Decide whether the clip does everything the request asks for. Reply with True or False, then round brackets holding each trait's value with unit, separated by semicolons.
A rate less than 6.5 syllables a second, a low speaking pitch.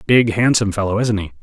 False (6.6 syllables/s; 110 Hz)